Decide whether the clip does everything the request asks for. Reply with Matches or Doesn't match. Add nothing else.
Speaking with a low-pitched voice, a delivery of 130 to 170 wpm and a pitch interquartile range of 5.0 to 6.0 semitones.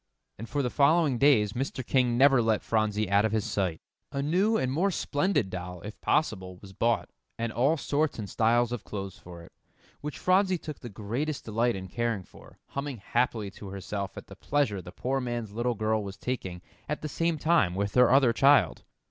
Doesn't match